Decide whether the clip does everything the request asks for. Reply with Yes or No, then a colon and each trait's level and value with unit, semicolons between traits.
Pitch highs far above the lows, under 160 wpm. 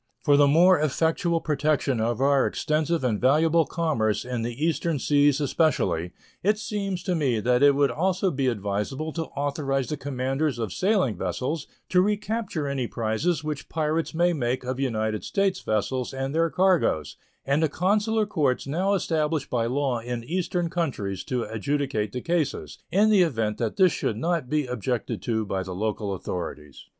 No: wide, 5.7 semitones; average, 170 wpm